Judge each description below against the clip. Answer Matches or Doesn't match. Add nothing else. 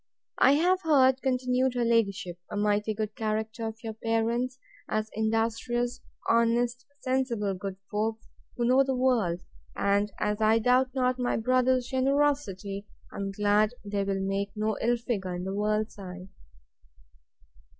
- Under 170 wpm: Matches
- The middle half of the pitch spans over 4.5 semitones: Doesn't match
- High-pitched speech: Matches